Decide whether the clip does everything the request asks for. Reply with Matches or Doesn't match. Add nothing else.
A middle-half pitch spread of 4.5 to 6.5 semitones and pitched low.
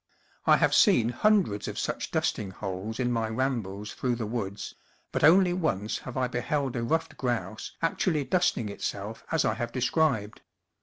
Matches